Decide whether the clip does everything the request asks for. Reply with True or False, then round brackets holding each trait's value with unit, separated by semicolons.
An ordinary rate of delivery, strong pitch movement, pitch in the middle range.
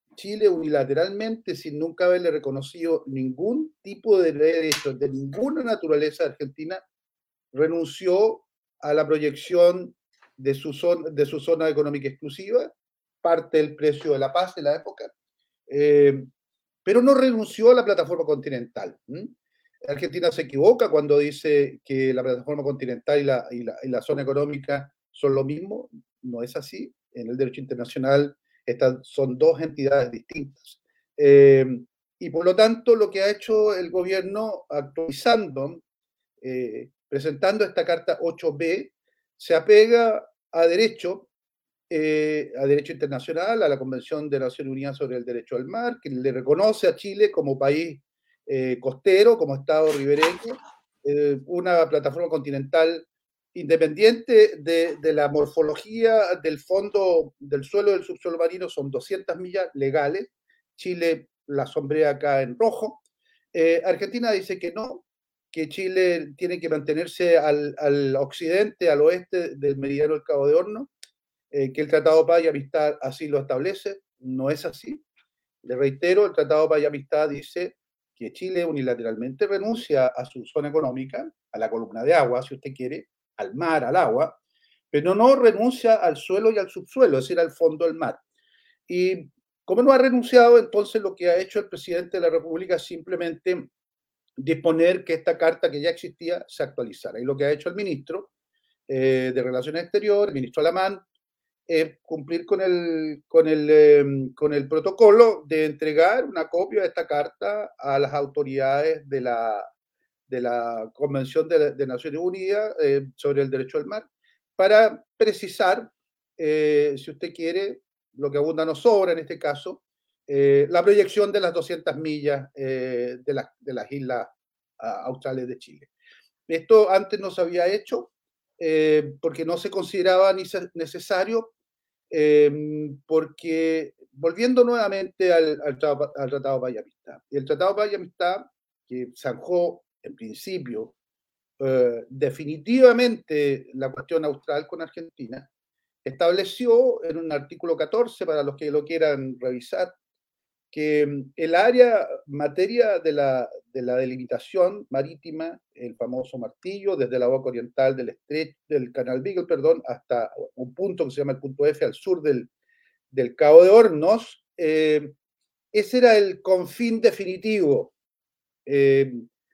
True (150 wpm; 6.4 semitones; 165 Hz)